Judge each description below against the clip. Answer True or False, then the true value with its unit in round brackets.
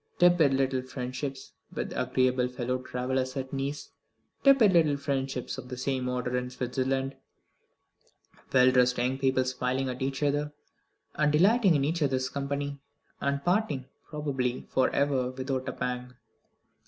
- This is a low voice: True (130 Hz)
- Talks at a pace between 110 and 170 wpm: True (140 wpm)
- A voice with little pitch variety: True (1.9 semitones)